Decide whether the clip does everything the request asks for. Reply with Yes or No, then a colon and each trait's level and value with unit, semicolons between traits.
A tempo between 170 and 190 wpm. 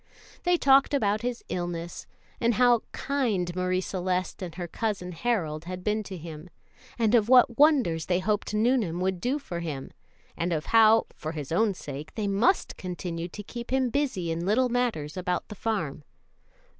Yes: average, 180 wpm